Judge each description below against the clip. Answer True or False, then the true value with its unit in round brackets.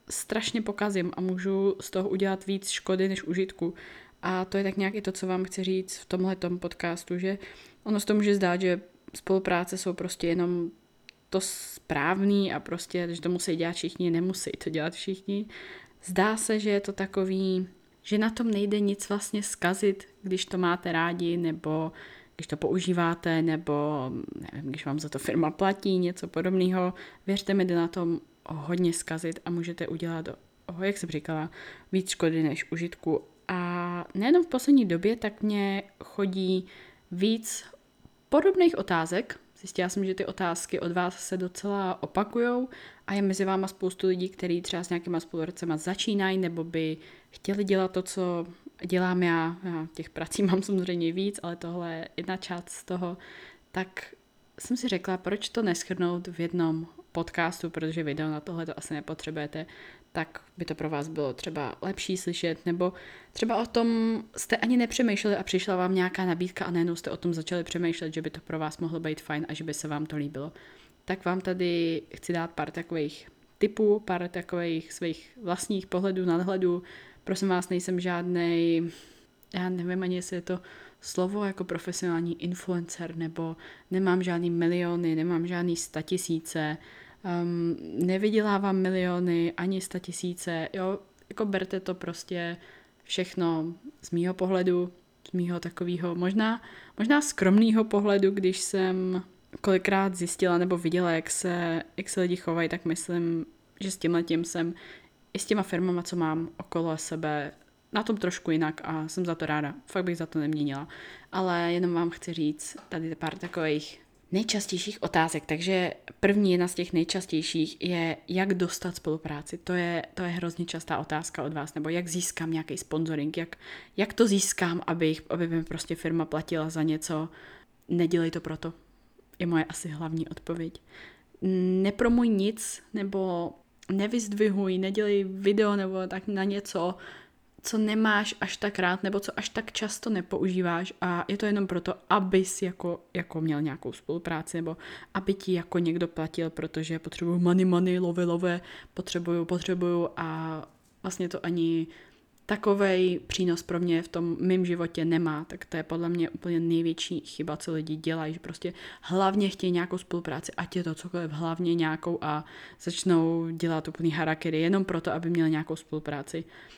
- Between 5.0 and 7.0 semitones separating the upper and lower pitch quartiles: False (2.4 semitones)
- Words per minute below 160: False (165 wpm)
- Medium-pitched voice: True (175 Hz)